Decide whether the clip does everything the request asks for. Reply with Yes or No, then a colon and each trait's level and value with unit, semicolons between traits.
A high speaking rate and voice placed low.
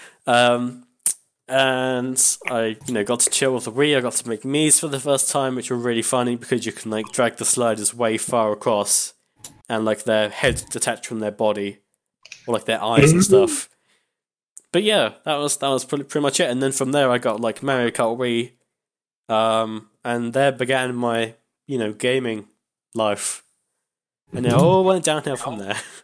No: average, 195 wpm; low, 125 Hz